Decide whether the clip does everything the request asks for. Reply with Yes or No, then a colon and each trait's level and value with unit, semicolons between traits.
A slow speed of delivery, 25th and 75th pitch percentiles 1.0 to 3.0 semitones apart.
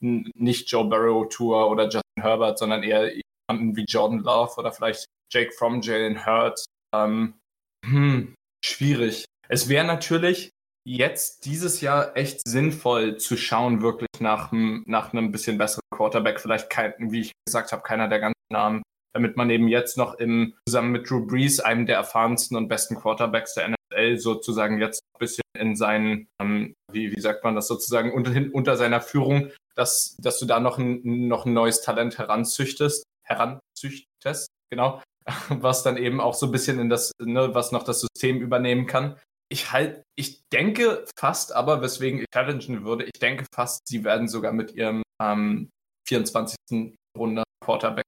No: average, 170 wpm; narrow, 2.5 semitones